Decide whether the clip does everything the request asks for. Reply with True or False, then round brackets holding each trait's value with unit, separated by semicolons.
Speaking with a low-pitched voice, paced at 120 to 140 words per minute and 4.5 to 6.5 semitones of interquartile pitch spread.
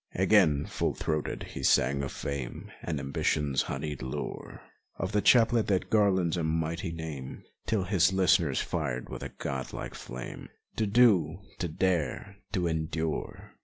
False (80 Hz; 150 wpm; 4.8 semitones)